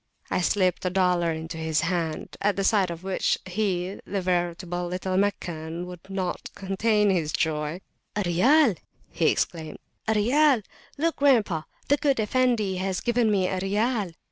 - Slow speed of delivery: No, average, 155 wpm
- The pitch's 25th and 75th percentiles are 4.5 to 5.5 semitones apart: No, average, 3.3 semitones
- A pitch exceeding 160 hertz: Yes, high, 190 Hz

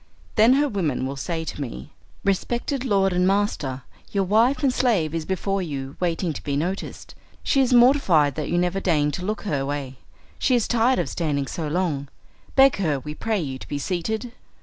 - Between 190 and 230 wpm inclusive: Yes, average, 195 wpm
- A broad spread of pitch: Yes, wide, 6.9 semitones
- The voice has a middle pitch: Yes, medium, 180 Hz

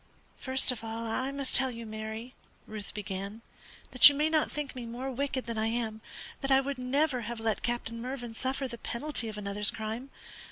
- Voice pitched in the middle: No, high, 240 Hz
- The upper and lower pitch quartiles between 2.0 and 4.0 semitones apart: Yes, average, 3.2 semitones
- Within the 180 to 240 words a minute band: Yes, average, 200 wpm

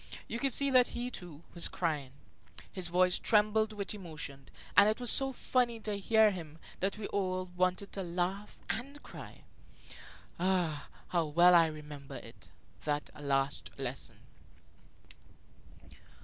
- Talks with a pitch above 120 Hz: Yes, medium, 185 Hz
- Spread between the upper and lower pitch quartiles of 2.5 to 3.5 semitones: No, average, 5.3 semitones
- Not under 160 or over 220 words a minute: No, average, 140 wpm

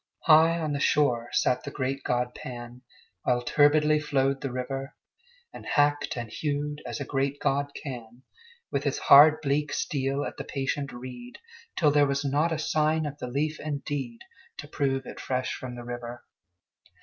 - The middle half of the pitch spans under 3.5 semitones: Yes, average, 2.8 semitones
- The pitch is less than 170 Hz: Yes, medium, 140 Hz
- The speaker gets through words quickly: No, average, 175 wpm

